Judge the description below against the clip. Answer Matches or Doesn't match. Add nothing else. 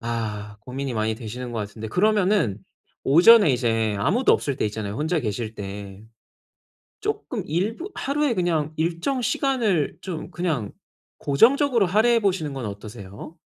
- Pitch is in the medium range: Matches